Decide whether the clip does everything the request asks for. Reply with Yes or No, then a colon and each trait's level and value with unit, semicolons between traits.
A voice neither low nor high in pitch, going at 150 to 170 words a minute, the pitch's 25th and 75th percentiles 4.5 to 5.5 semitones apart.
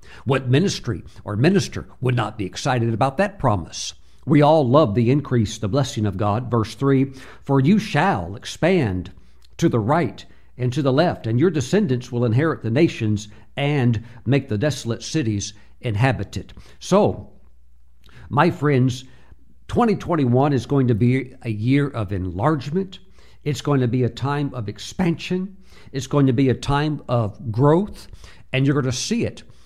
No: low, 125 Hz; average, 160 wpm; average, 5.2 semitones